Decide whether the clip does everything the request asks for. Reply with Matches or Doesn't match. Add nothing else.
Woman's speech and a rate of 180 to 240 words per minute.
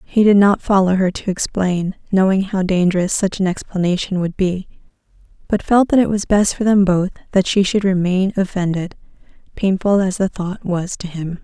Matches